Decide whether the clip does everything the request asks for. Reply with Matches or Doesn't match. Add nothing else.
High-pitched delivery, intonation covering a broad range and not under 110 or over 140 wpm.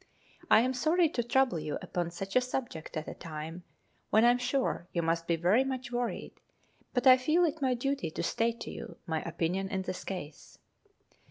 Doesn't match